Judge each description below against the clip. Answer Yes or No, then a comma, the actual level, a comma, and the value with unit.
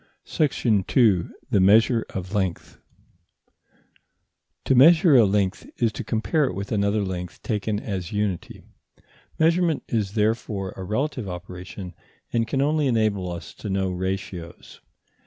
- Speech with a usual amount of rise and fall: Yes, average, 3.9 semitones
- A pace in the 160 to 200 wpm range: No, slow, 135 wpm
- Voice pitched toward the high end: No, low, 105 Hz